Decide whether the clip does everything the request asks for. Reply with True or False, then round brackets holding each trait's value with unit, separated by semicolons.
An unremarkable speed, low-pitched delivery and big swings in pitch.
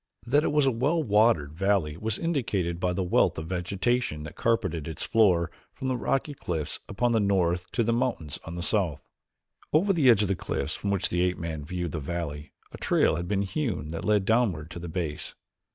False (215 wpm; 95 Hz; 5.7 semitones)